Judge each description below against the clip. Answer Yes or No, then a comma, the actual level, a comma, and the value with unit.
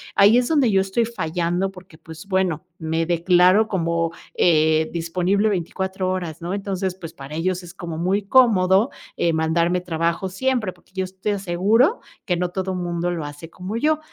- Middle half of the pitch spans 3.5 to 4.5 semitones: No, narrow, 2.6 semitones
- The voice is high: No, medium, 180 Hz